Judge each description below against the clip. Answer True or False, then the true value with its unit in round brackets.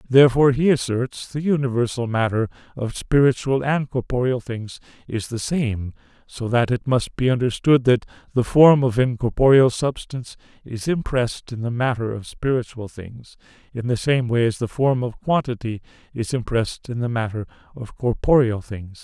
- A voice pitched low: True (125 Hz)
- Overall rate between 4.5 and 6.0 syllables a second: True (5.0 syllables/s)